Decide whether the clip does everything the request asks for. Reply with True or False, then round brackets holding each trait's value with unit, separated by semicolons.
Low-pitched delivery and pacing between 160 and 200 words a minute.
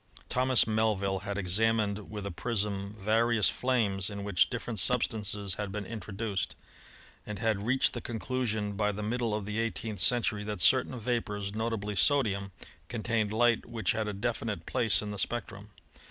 True (105 Hz; 165 wpm)